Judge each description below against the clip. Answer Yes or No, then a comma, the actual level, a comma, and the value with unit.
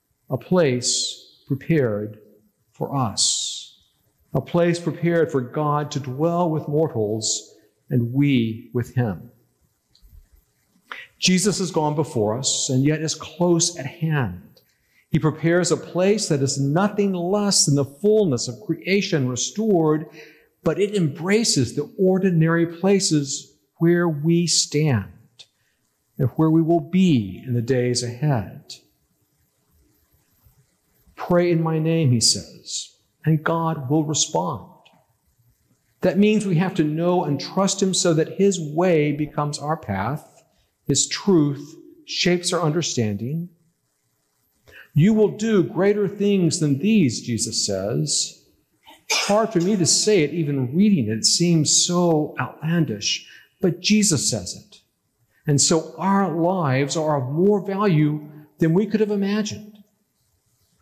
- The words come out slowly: Yes, slow, 130 wpm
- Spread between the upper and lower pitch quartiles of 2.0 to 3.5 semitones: No, wide, 5.4 semitones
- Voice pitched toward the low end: No, medium, 155 Hz